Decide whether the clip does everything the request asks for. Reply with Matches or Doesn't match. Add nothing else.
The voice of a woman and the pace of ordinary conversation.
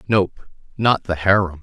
Doesn't match